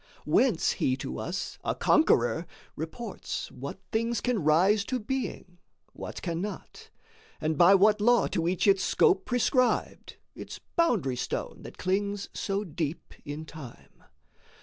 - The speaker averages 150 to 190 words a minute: No, slow, 135 wpm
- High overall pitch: Yes, high, 195 Hz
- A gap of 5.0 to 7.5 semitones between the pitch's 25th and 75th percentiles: Yes, wide, 5.6 semitones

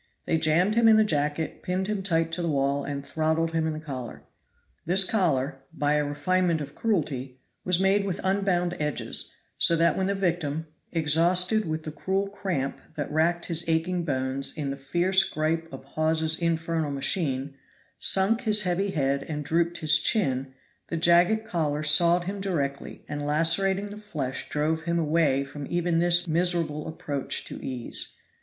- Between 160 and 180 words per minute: Yes, average, 170 wpm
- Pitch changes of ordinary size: Yes, average, 3.6 semitones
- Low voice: No, medium, 165 Hz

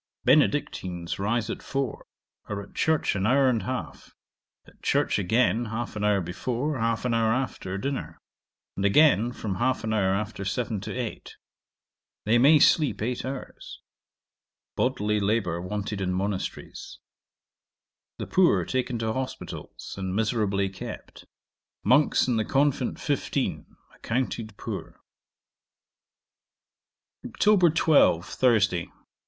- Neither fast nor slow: No, slow, 125 wpm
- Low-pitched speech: Yes, low, 110 Hz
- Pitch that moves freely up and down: No, average, 4.5 semitones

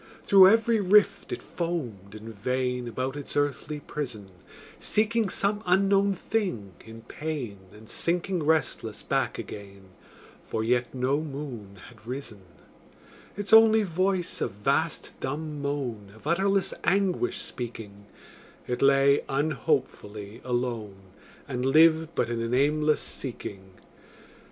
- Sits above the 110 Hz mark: Yes, medium, 140 Hz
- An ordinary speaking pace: No, slow, 120 wpm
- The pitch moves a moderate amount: No, wide, 7.4 semitones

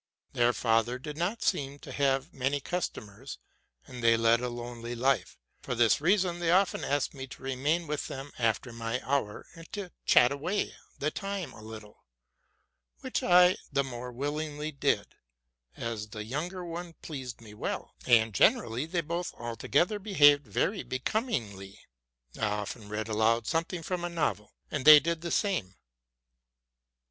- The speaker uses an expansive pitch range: Yes, wide, 6.3 semitones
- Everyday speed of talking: Yes, average, 155 wpm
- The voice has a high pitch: No, low, 135 Hz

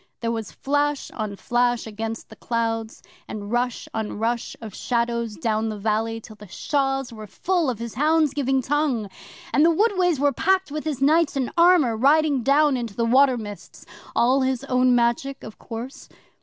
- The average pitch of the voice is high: Yes, high, 245 Hz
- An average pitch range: Yes, average, 4.2 semitones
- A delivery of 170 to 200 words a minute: Yes, average, 180 wpm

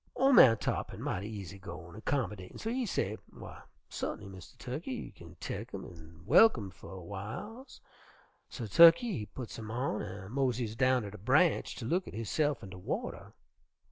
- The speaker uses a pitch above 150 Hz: No, low, 110 Hz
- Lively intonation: Yes, wide, 6.7 semitones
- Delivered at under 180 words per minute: No, average, 185 wpm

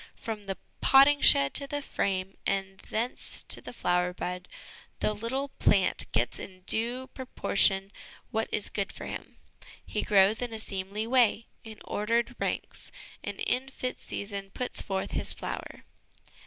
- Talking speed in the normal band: Yes, average, 155 wpm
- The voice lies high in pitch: Yes, high, 210 Hz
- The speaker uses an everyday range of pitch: Yes, average, 4.1 semitones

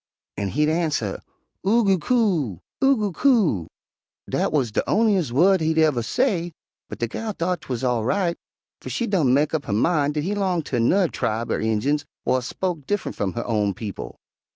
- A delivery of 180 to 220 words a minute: Yes, average, 190 wpm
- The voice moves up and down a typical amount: No, wide, 8.3 semitones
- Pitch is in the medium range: Yes, medium, 155 Hz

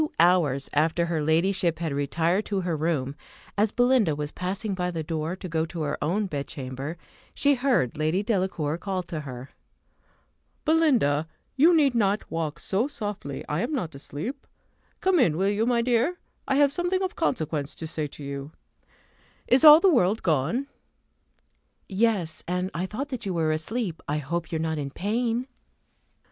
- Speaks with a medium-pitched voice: Yes, medium, 180 Hz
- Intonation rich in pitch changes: Yes, wide, 7.0 semitones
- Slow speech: No, average, 175 wpm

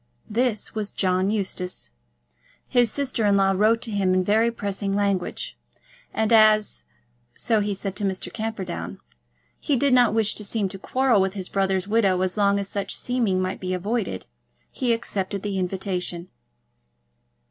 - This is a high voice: Yes, high, 200 Hz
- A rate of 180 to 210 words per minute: No, average, 160 wpm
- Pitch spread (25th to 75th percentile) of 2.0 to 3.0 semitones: Yes, average, 2.7 semitones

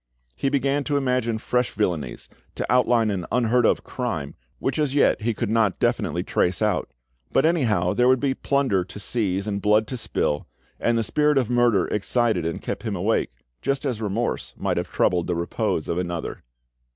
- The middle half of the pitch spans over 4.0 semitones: Yes, average, 4.5 semitones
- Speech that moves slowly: No, average, 190 wpm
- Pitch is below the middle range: Yes, low, 115 Hz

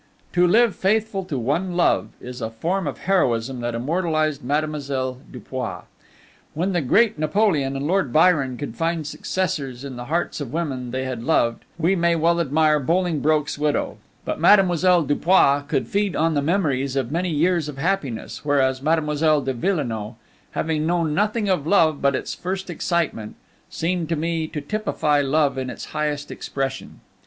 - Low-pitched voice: No, medium, 155 Hz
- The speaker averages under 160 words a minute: No, average, 165 wpm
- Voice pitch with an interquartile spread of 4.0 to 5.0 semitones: Yes, average, 4.3 semitones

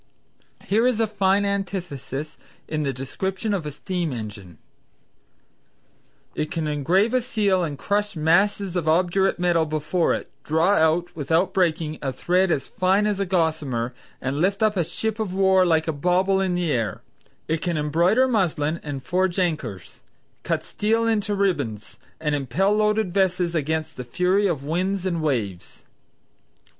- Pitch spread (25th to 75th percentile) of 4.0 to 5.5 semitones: Yes, average, 4.3 semitones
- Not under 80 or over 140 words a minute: No, average, 160 wpm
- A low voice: No, medium, 175 Hz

